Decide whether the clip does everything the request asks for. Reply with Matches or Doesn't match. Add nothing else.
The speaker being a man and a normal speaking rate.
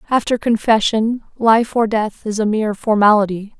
Doesn't match